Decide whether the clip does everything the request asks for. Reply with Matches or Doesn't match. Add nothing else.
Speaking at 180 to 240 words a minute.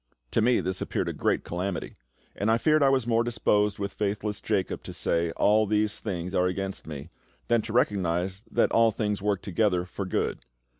Matches